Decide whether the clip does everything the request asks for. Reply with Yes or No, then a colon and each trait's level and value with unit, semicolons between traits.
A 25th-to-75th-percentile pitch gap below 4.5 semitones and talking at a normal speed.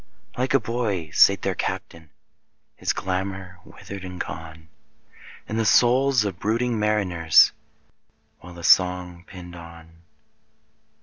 No: average, 4.0 semitones; slow, 130 wpm